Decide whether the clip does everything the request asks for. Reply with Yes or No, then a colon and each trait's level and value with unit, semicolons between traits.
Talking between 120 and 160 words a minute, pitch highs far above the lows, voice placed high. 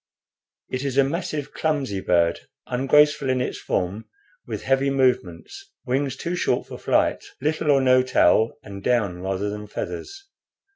No: average, 150 wpm; wide, 5.9 semitones; low, 130 Hz